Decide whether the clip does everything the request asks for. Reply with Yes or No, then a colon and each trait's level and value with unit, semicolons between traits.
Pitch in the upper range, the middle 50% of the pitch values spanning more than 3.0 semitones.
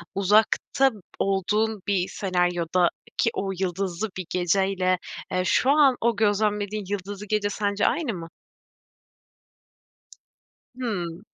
No: high, 200 Hz; average, 2.7 semitones